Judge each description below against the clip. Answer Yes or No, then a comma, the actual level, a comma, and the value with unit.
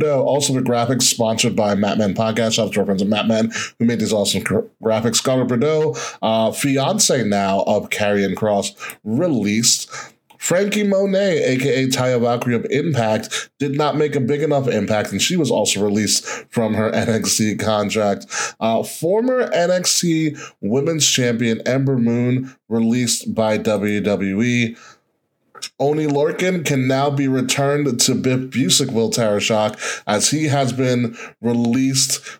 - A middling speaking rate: Yes, average, 145 wpm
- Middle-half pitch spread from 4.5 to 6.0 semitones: No, average, 4.1 semitones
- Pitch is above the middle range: No, low, 120 Hz